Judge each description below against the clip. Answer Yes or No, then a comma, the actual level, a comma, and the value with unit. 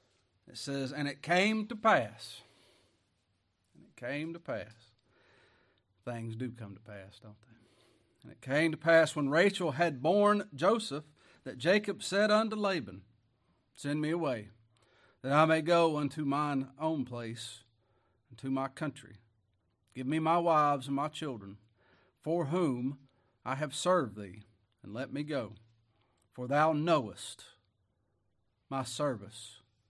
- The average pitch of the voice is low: Yes, low, 125 Hz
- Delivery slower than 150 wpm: Yes, average, 140 wpm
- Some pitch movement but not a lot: No, wide, 6.1 semitones